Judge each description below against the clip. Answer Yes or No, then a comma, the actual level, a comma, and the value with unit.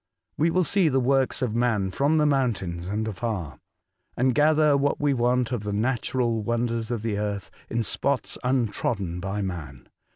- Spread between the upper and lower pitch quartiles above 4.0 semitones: Yes, average, 4.6 semitones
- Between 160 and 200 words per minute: Yes, average, 170 wpm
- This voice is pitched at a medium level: No, low, 120 Hz